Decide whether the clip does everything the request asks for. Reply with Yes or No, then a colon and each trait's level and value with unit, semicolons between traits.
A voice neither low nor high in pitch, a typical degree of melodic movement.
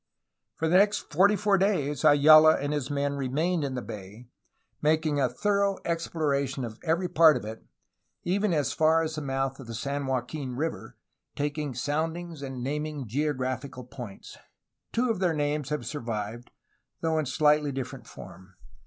Yes: medium, 145 Hz; average, 3.5 semitones